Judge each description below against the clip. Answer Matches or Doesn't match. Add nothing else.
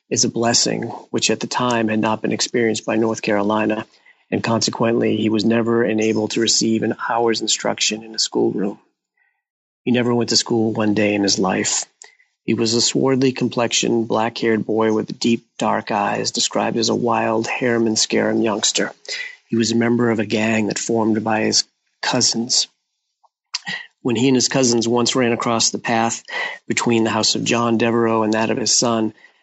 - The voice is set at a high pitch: Doesn't match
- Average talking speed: Matches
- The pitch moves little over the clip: Matches